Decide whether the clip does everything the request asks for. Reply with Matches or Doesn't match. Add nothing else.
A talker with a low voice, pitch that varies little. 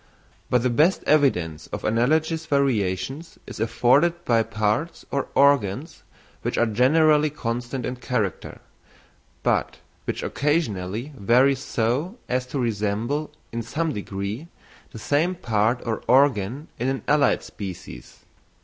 Doesn't match